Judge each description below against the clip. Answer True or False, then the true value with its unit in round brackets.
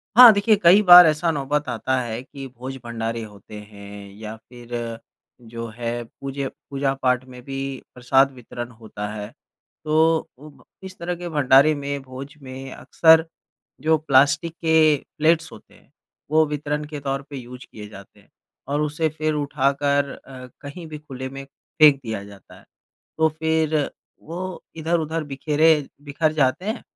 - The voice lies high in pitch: False (140 Hz)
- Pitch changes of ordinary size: True (3.7 semitones)